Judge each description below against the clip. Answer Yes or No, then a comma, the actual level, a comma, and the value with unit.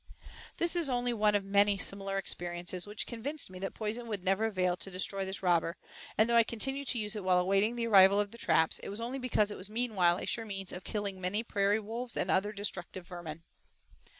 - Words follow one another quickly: Yes, fast, 225 wpm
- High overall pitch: Yes, high, 205 Hz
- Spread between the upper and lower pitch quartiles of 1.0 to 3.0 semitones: No, average, 3.4 semitones